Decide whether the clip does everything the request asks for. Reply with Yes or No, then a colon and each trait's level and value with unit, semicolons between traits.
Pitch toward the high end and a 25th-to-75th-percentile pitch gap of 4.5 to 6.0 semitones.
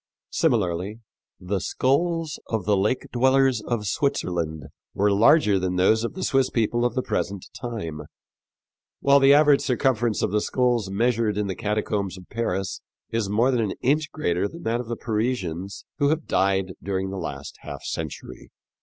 No: low, 110 Hz; average, 4.9 semitones